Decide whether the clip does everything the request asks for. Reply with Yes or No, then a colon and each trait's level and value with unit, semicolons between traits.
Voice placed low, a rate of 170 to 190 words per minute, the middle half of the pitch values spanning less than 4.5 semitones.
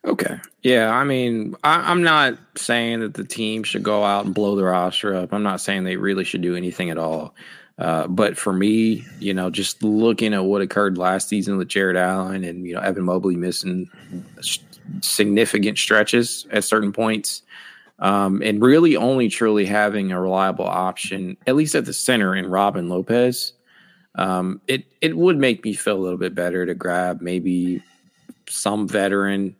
Yes: low, 100 Hz; average, 180 wpm; average, 3.2 semitones